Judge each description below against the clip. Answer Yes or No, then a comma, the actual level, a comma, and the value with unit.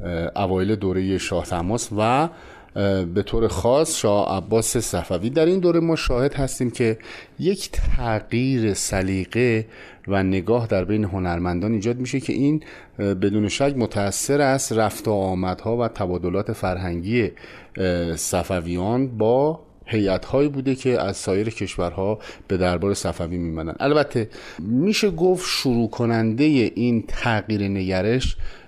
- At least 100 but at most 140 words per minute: Yes, average, 125 wpm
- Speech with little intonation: No, average, 4.6 semitones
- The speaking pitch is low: Yes, low, 110 Hz